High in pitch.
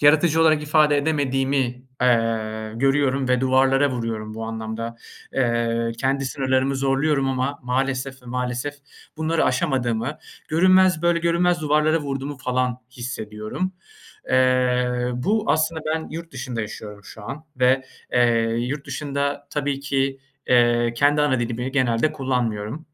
No: low, 135 Hz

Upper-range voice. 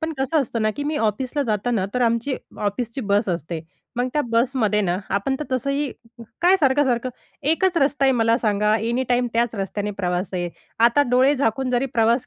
Yes: high, 235 Hz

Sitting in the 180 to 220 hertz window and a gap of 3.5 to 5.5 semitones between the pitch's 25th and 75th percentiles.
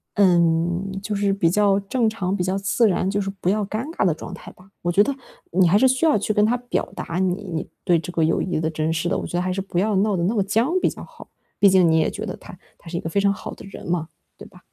No: high, 190 Hz; average, 3.1 semitones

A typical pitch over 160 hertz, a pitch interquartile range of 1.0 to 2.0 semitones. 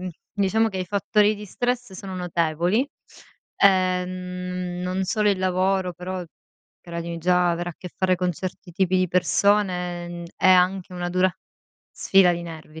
Yes: medium, 185 Hz; narrow, 1.4 semitones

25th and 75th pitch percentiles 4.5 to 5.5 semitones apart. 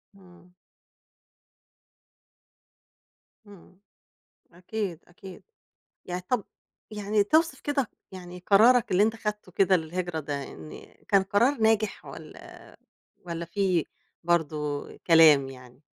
No: average, 4.1 semitones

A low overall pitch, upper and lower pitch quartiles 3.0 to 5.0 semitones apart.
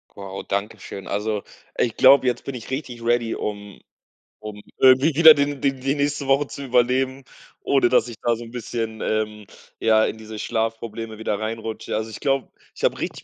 Yes: low, 115 Hz; average, 3.4 semitones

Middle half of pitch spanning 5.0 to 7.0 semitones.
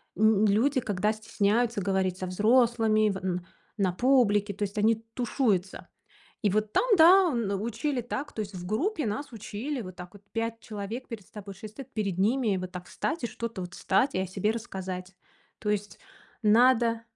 No: average, 3.4 semitones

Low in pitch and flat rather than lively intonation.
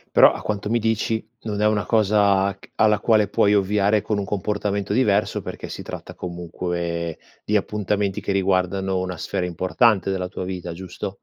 Yes: low, 100 Hz; narrow, 2.3 semitones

